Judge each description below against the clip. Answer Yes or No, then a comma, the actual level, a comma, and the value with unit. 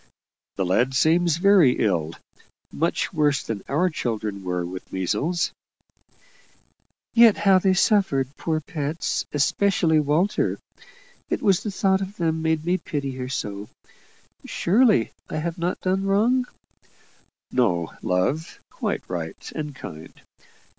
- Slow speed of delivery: Yes, slow, 125 wpm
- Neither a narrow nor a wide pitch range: No, wide, 7.8 semitones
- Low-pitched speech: No, medium, 155 Hz